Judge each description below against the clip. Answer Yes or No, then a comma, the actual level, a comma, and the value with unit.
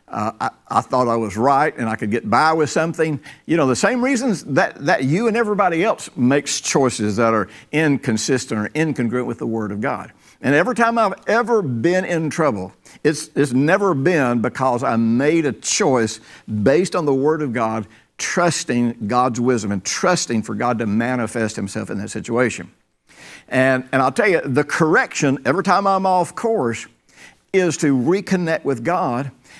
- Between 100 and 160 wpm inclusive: No, average, 180 wpm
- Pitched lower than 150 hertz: Yes, medium, 140 Hz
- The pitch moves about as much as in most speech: No, wide, 6.7 semitones